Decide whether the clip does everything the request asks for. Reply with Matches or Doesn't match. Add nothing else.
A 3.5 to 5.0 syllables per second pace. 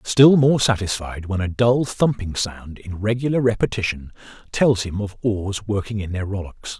Matches